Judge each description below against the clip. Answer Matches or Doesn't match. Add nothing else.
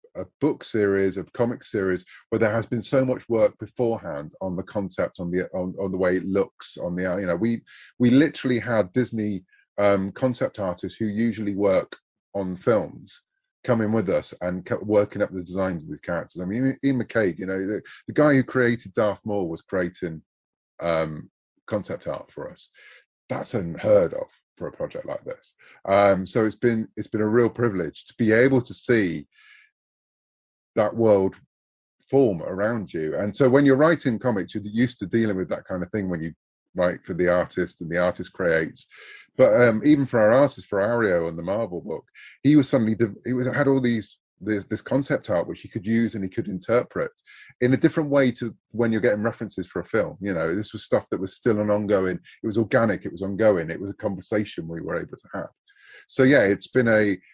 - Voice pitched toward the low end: Matches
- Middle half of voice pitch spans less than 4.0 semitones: Doesn't match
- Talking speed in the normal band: Doesn't match